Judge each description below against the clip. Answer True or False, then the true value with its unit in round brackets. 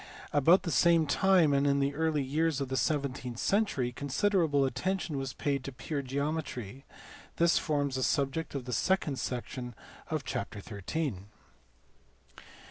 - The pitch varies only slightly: False (3.7 semitones)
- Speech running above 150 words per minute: False (145 wpm)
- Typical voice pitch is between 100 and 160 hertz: True (140 Hz)